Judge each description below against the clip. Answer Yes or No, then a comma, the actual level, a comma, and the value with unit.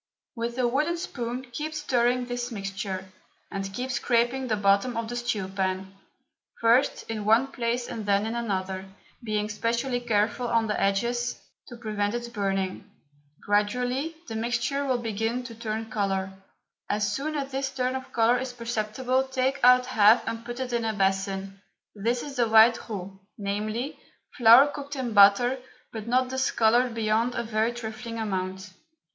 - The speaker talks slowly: No, average, 165 wpm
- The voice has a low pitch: No, high, 230 Hz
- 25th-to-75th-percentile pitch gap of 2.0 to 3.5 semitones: Yes, average, 3.1 semitones